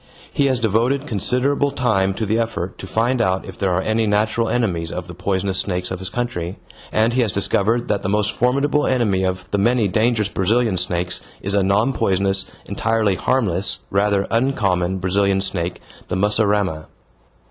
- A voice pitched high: No, low, 100 Hz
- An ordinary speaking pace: Yes, average, 175 wpm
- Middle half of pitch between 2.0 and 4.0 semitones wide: Yes, average, 3.6 semitones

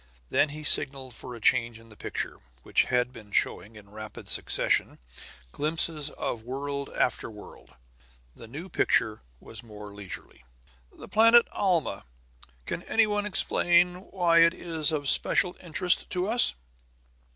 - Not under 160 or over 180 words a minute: No, average, 145 wpm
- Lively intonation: Yes, wide, 7.5 semitones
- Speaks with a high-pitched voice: No, medium, 145 Hz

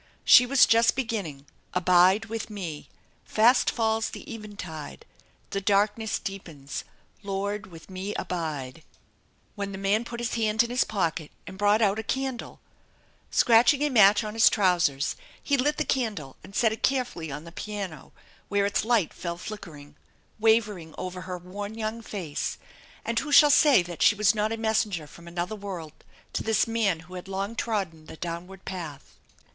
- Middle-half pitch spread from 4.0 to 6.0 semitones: Yes, average, 4.3 semitones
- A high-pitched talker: Yes, high, 200 Hz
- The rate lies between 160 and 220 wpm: Yes, average, 170 wpm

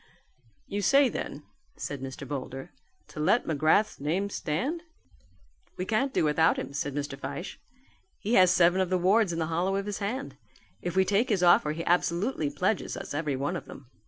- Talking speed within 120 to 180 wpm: No, average, 190 wpm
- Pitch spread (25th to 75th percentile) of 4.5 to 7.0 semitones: Yes, average, 5.1 semitones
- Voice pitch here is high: No, medium, 175 Hz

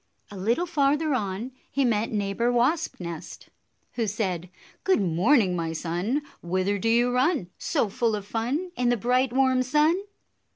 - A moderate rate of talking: Yes, average, 160 wpm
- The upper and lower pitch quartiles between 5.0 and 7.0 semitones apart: Yes, average, 5.3 semitones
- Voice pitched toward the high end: Yes, high, 235 Hz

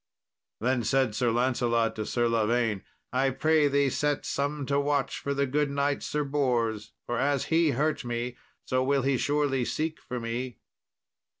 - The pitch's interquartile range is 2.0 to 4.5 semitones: Yes, average, 3.0 semitones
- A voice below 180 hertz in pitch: Yes, low, 135 Hz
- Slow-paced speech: No, average, 170 wpm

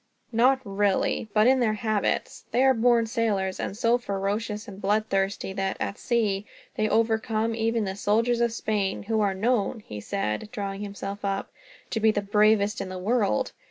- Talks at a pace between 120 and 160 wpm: No, average, 180 wpm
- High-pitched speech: Yes, high, 215 Hz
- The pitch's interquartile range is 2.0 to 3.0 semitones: Yes, narrow, 2.4 semitones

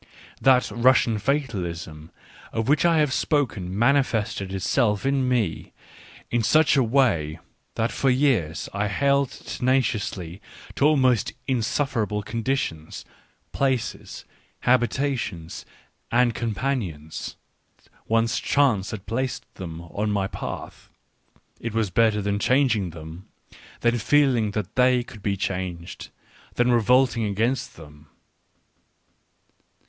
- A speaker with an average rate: No, slow, 115 wpm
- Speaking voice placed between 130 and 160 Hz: No, low, 115 Hz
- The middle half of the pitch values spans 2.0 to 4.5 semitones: No, average, 5.0 semitones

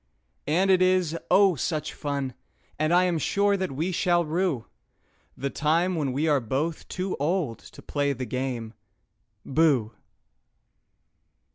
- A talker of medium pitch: Yes, medium, 155 Hz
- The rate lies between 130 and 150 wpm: Yes, slow, 135 wpm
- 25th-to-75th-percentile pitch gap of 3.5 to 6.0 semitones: Yes, average, 5.0 semitones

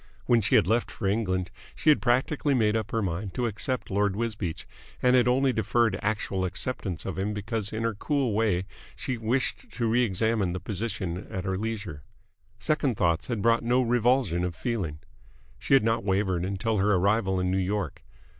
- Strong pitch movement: No, average, 3.7 semitones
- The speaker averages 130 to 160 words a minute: No, average, 190 wpm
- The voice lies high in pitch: No, low, 105 Hz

